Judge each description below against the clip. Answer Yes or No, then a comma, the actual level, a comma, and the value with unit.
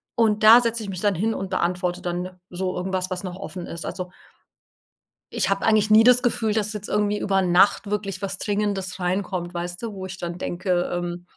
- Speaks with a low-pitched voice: No, high, 190 Hz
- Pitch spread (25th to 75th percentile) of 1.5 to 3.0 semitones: Yes, average, 2.7 semitones